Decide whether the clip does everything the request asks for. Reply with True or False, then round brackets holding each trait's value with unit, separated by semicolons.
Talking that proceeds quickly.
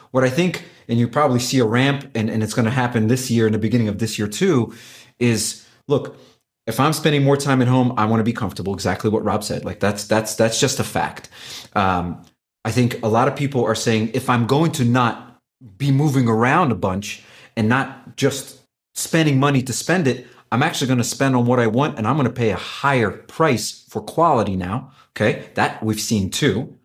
True (225 wpm)